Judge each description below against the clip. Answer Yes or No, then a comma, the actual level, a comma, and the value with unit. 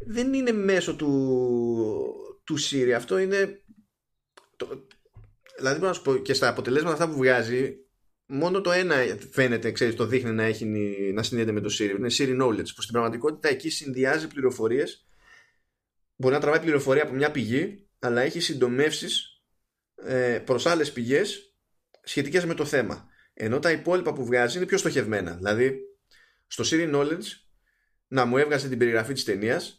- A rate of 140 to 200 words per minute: Yes, average, 150 wpm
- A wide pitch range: Yes, wide, 7.1 semitones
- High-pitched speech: No, medium, 140 Hz